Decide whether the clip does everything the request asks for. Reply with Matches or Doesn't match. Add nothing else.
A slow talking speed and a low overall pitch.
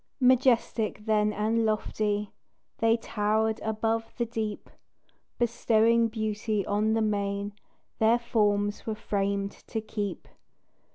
Doesn't match